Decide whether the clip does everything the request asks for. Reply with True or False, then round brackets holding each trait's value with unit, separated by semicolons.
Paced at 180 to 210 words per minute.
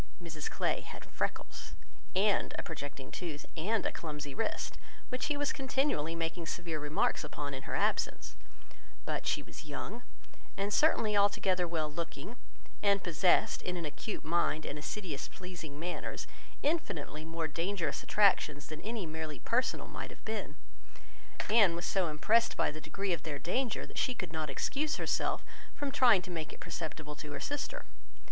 False (165 wpm)